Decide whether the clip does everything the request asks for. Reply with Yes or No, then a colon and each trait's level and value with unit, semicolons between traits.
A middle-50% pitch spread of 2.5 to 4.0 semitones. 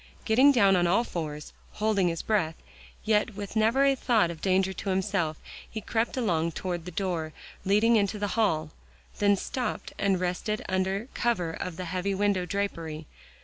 Yes: average, 3.6 semitones